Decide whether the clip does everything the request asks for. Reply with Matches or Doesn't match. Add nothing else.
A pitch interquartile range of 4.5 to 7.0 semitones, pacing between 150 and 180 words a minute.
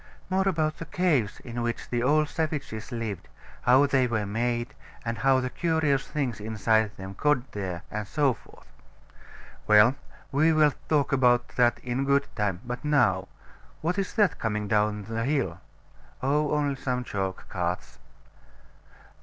Matches